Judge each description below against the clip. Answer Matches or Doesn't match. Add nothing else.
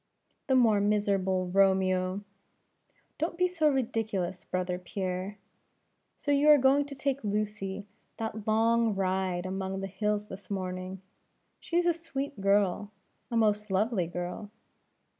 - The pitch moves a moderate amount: Matches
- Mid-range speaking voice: Doesn't match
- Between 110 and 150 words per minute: Matches